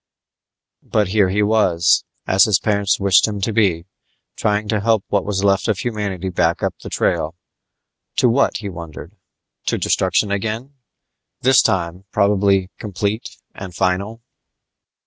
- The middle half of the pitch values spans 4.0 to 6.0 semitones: No, narrow, 2.4 semitones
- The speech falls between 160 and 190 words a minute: No, average, 145 wpm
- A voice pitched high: No, low, 100 Hz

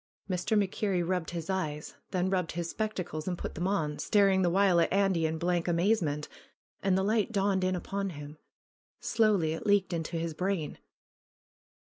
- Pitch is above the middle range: No, medium, 180 Hz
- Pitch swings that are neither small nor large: Yes, average, 3.0 semitones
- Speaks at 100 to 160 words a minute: No, average, 175 wpm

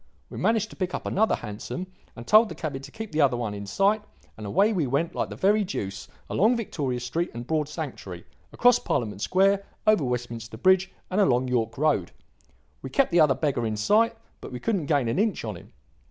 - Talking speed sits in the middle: No, fast, 210 wpm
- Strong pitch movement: Yes, wide, 8.8 semitones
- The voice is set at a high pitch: No, medium, 150 Hz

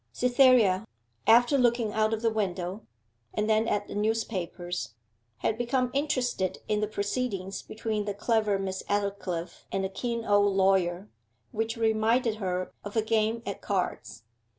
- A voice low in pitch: No, high, 215 Hz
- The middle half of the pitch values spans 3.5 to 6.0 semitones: No, average, 2.8 semitones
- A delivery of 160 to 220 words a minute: No, average, 150 wpm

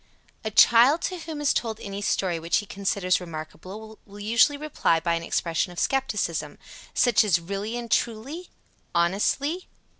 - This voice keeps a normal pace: Yes, average, 160 wpm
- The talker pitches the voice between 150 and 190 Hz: No, high, 205 Hz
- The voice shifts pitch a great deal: Yes, wide, 5.7 semitones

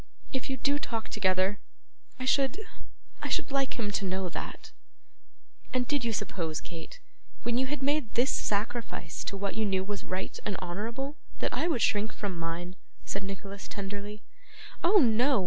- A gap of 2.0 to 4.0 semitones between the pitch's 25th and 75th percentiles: No, average, 5.3 semitones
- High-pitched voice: Yes, high, 210 Hz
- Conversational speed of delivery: Yes, average, 170 wpm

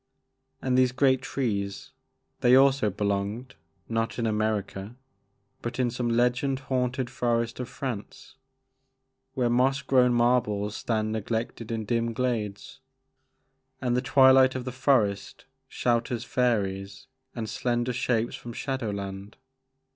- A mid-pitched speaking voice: No, low, 120 Hz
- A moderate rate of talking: No, slow, 130 wpm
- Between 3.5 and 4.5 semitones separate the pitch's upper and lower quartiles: No, average, 2.9 semitones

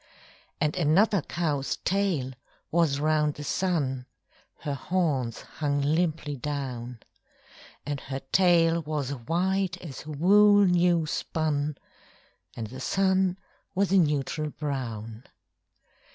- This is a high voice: No, medium, 150 Hz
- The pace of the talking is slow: Yes, slow, 110 wpm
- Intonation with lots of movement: No, average, 4.2 semitones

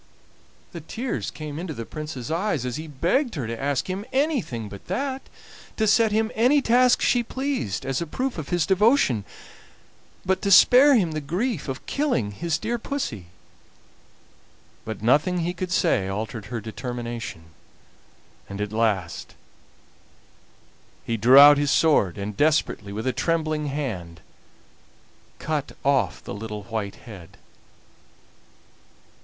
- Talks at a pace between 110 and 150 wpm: Yes, average, 140 wpm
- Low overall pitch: No, medium, 145 Hz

